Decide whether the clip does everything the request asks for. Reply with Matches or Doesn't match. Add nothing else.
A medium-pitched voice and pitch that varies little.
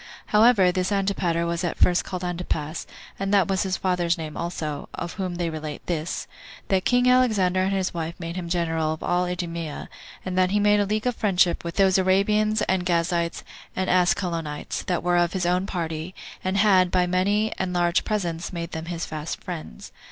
Matches